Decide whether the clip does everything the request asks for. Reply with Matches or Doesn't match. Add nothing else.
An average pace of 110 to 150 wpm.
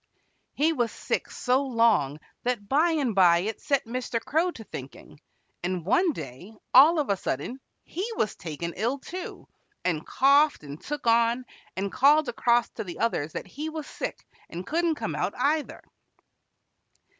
Doesn't match